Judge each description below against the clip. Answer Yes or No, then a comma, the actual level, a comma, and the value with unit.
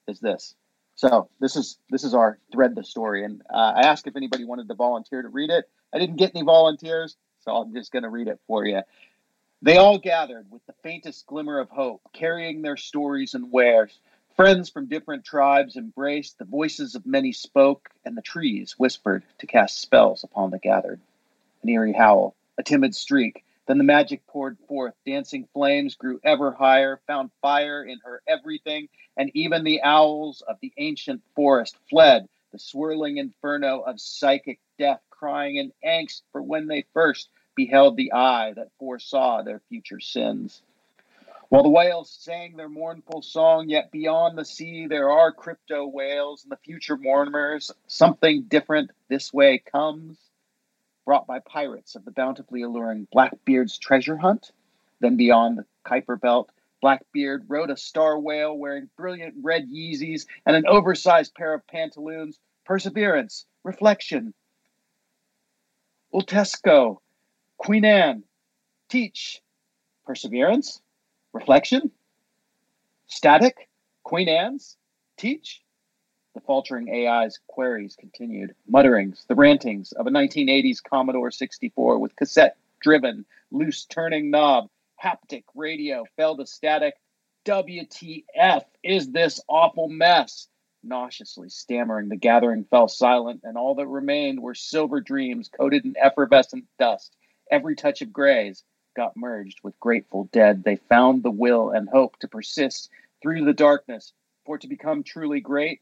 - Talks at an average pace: Yes, average, 150 wpm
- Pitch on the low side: No, medium, 155 Hz